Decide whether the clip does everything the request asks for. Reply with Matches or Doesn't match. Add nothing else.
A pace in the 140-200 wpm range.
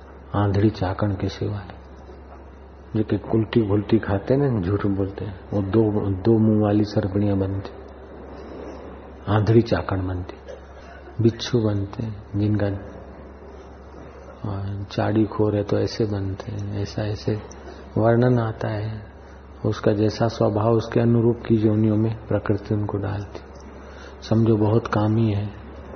Doesn't match